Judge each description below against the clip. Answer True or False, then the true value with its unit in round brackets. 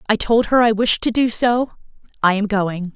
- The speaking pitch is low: False (220 Hz)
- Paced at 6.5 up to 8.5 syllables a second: False (4.9 syllables/s)